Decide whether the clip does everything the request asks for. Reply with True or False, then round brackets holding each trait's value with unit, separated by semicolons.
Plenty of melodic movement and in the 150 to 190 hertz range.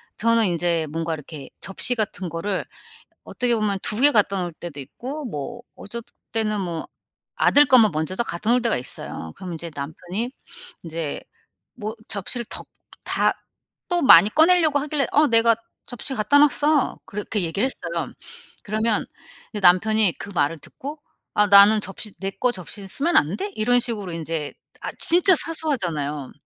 False (6.4 semitones; 210 Hz)